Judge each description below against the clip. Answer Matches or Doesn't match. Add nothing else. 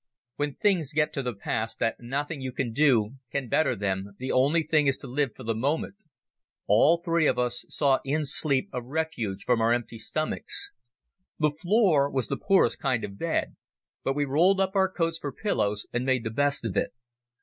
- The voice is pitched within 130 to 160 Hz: Matches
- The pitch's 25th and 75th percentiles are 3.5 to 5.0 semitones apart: Matches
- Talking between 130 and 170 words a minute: Doesn't match